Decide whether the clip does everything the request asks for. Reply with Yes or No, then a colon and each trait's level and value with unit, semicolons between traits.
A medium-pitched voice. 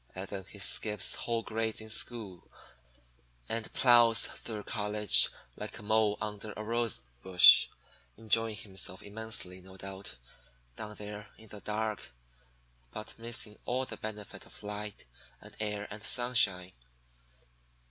No: low, 105 Hz